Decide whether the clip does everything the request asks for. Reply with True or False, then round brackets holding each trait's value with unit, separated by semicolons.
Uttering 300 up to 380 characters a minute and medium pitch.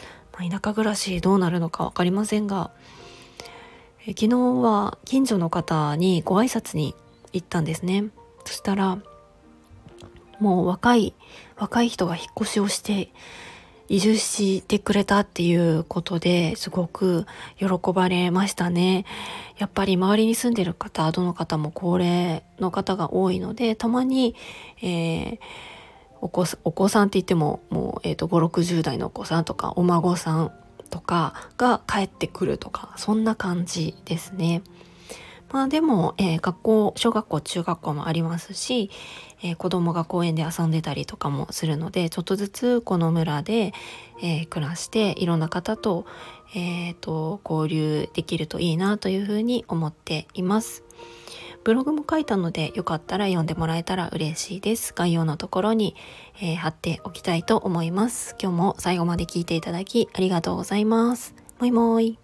True (305 characters per minute; 180 Hz)